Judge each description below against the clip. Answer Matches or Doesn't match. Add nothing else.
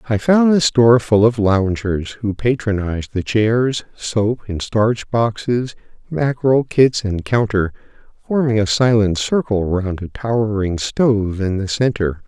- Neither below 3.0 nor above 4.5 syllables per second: Matches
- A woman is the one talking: Doesn't match